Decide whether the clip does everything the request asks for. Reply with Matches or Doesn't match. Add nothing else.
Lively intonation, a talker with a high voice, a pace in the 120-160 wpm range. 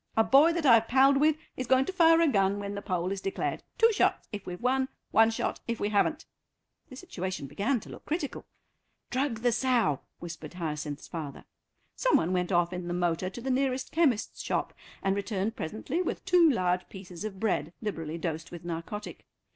Doesn't match